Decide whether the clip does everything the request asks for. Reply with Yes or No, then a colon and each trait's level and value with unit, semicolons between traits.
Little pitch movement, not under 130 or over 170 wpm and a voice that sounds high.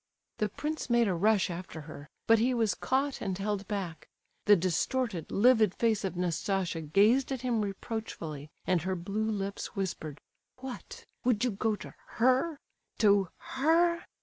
No: average, 4.7 semitones; average, 150 wpm; high, 210 Hz